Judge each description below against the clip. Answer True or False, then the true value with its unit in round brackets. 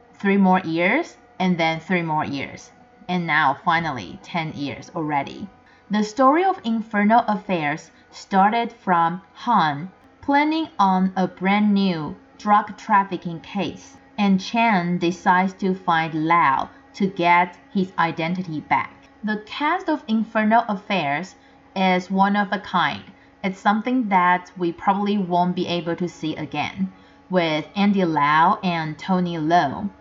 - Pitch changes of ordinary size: True (3.5 semitones)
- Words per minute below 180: True (135 wpm)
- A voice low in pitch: False (185 Hz)